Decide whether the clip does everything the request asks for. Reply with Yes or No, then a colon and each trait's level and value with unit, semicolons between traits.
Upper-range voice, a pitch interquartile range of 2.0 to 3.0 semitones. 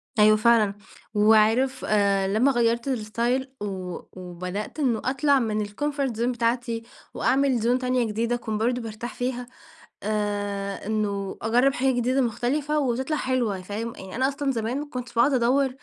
No: high, 235 Hz; average, 3.4 semitones